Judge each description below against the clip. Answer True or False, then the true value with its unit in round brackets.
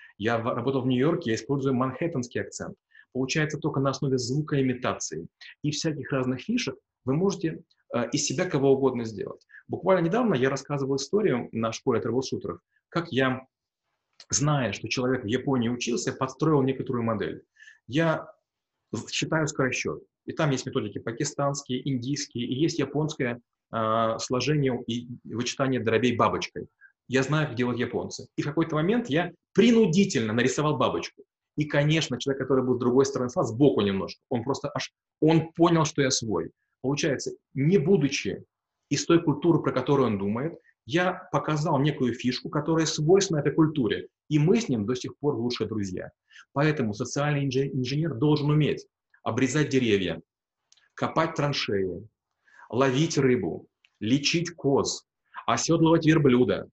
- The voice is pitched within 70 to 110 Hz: False (135 Hz)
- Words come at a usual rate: True (145 wpm)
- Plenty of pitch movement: False (3.7 semitones)